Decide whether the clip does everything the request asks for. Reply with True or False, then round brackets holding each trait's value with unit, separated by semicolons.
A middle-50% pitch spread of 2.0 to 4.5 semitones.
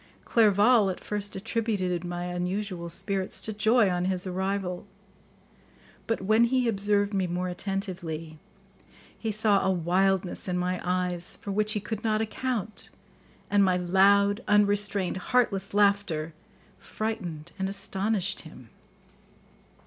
True (2.6 semitones)